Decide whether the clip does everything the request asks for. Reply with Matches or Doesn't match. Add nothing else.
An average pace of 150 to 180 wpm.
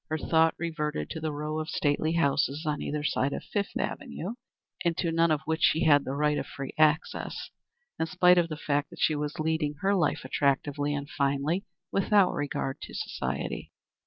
Doesn't match